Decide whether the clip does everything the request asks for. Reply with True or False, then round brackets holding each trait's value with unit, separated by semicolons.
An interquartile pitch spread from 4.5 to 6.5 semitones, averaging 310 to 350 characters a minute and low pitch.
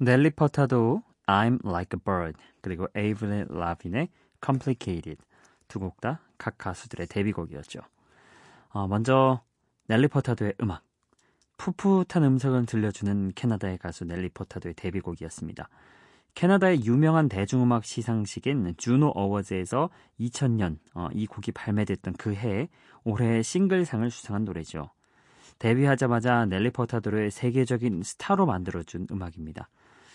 True (5.4 semitones; 330 characters per minute; 110 Hz)